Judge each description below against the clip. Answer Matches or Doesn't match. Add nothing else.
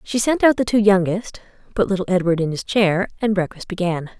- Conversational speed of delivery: Doesn't match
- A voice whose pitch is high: Matches